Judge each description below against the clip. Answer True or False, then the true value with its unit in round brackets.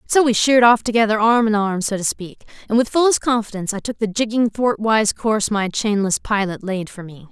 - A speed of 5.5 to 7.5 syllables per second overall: True (5.8 syllables/s)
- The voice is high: True (215 Hz)